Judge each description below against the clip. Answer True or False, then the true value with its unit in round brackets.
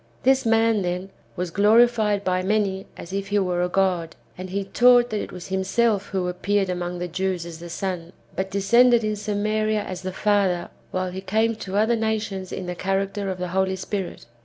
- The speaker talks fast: True (210 wpm)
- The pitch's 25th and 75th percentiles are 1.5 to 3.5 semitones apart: True (2.7 semitones)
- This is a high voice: True (195 Hz)